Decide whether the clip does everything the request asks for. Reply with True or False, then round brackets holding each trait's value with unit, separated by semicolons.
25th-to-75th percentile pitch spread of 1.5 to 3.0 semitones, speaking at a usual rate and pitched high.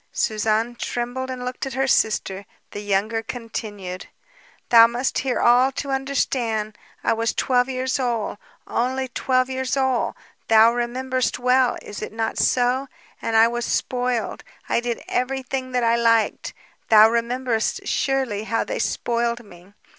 True (2.4 semitones; 145 wpm; 240 Hz)